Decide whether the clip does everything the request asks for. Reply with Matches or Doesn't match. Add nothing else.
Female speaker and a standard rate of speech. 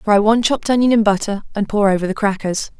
Doesn't match